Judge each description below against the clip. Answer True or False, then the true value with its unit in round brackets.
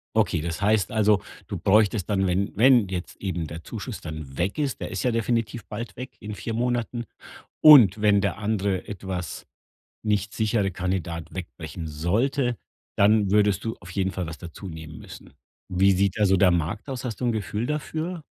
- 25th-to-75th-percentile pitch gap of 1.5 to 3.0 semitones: False (3.8 semitones)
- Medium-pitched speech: False (100 Hz)